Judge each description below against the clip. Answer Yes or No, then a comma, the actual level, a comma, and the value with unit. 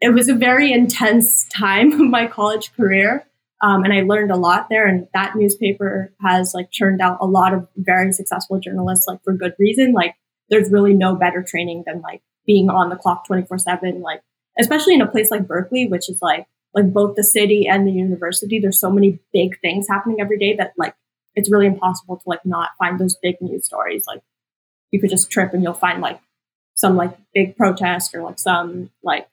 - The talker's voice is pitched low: No, high, 195 Hz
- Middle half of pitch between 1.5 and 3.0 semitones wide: Yes, narrow, 2.4 semitones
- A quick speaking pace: Yes, fast, 210 wpm